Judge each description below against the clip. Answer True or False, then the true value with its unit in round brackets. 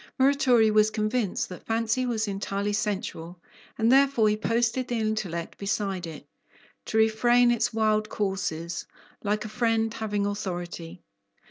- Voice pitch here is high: True (215 Hz)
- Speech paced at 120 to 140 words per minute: True (135 wpm)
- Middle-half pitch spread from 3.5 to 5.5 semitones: False (2.5 semitones)